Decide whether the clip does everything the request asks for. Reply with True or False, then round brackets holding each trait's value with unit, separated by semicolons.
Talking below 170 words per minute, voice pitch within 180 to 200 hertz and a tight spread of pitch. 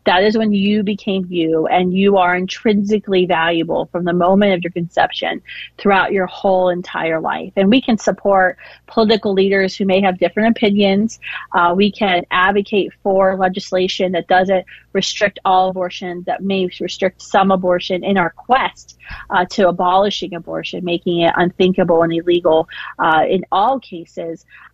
True (160 wpm; 185 Hz; 2.2 semitones)